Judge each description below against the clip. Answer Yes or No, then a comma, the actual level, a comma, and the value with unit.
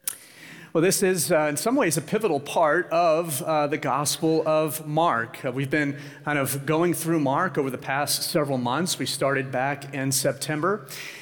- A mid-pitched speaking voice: Yes, medium, 150 Hz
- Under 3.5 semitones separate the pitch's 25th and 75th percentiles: Yes, average, 2.9 semitones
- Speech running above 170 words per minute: Yes, average, 180 wpm